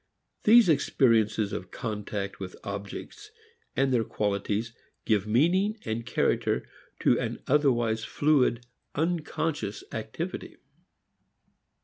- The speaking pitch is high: No, low, 120 Hz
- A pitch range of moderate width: No, wide, 6.8 semitones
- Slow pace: Yes, slow, 90 wpm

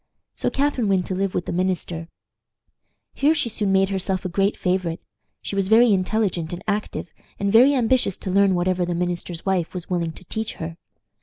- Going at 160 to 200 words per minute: Yes, average, 190 wpm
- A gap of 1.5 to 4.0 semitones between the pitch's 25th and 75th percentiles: Yes, average, 3.0 semitones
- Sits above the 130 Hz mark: Yes, high, 190 Hz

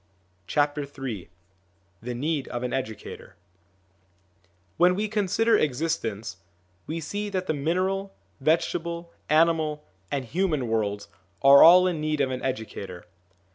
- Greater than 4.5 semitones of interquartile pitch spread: Yes, average, 5.2 semitones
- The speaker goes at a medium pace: No, slow, 120 wpm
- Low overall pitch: No, medium, 150 Hz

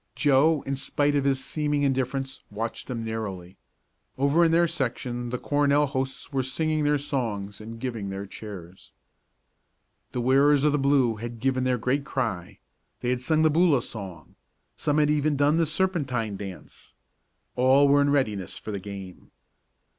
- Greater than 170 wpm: No, average, 165 wpm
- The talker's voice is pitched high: No, low, 130 Hz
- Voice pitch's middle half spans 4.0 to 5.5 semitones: Yes, average, 4.5 semitones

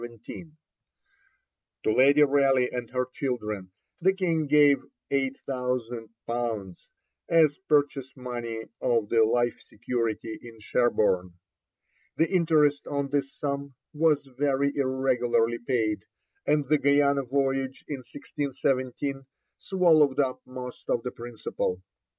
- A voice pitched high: No, low, 130 Hz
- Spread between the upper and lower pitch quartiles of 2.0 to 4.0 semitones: Yes, average, 3.1 semitones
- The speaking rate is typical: No, slow, 110 wpm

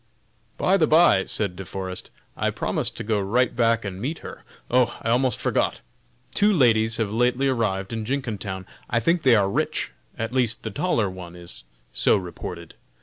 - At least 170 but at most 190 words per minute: Yes, average, 180 wpm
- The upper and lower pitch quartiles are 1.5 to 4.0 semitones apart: No, average, 4.8 semitones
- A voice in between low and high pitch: No, low, 115 Hz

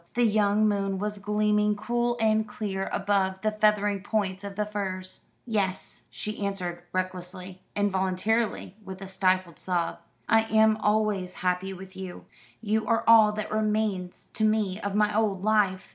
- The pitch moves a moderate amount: No, narrow, 2.2 semitones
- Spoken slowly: No, average, 155 wpm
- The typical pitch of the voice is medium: No, high, 205 Hz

